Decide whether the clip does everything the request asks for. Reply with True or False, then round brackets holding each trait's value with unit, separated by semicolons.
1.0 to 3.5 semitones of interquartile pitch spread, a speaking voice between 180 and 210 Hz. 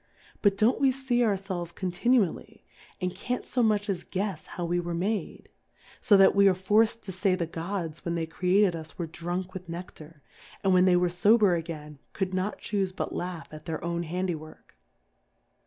True (3.1 semitones; 185 Hz)